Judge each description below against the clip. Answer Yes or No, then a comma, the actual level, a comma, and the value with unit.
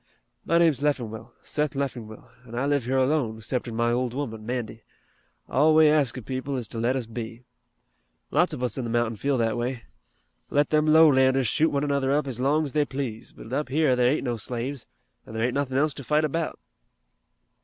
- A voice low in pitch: Yes, low, 130 Hz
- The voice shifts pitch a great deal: No, average, 3.5 semitones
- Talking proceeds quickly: Yes, fast, 210 wpm